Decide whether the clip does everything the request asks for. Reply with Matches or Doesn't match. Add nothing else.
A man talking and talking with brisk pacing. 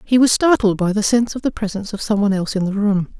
Doesn't match